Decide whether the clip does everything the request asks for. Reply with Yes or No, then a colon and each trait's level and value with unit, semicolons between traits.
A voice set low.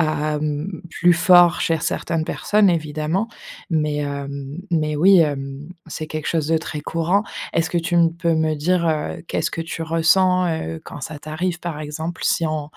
No: medium, 160 Hz